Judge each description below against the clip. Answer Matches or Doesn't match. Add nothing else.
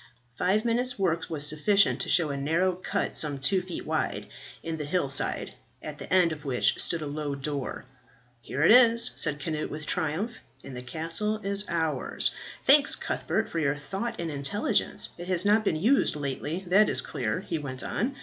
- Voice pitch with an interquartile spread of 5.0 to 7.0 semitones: Matches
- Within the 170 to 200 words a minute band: Matches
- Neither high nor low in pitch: Matches